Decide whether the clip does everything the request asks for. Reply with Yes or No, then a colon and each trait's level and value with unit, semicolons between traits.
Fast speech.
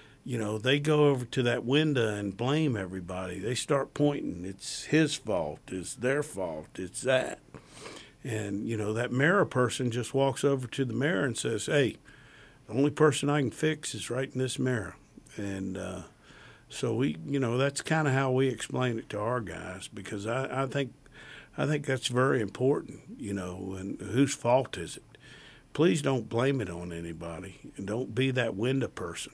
No: average, 185 wpm